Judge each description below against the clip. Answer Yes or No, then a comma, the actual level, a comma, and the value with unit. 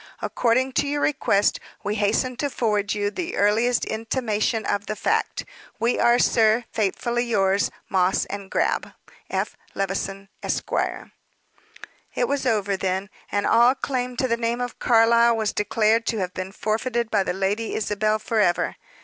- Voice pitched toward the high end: Yes, high, 220 Hz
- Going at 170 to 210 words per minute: No, average, 155 wpm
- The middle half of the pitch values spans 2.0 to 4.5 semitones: Yes, average, 2.8 semitones